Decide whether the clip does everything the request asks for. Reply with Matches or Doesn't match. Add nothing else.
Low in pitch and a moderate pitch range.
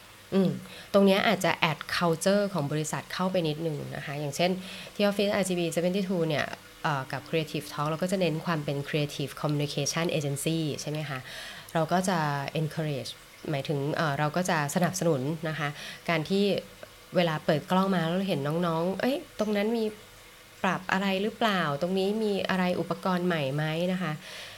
Doesn't match